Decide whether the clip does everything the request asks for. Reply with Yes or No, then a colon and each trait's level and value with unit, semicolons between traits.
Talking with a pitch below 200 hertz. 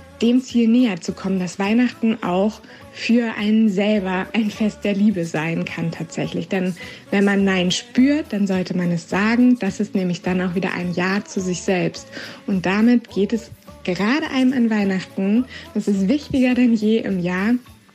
No: high, 205 Hz